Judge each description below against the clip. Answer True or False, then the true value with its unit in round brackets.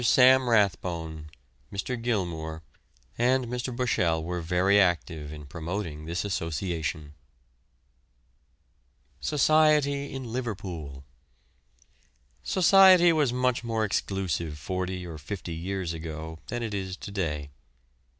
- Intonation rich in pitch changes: True (7.0 semitones)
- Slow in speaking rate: True (105 wpm)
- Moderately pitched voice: False (95 Hz)